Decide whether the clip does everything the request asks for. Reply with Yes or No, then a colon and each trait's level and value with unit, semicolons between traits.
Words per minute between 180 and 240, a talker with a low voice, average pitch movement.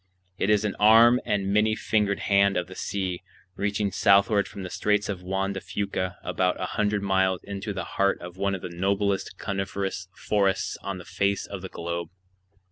No: average, 190 wpm; low, 100 Hz; narrow, 1.4 semitones